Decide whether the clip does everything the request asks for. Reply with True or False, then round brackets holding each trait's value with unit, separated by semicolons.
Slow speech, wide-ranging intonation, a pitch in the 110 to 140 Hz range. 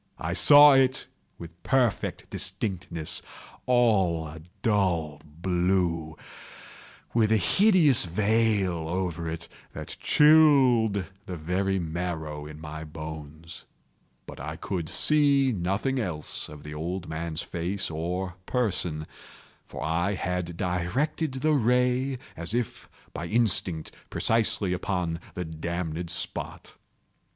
False (110 wpm; 5.7 semitones; 90 Hz)